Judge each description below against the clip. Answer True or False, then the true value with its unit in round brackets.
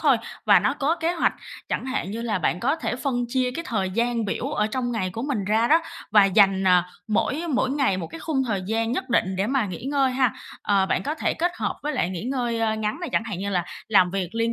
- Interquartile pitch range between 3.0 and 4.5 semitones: False (5.2 semitones)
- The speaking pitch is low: False (230 Hz)